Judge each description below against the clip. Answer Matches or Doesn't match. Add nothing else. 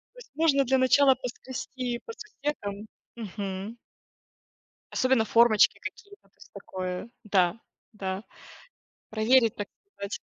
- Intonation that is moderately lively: Matches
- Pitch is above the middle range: Matches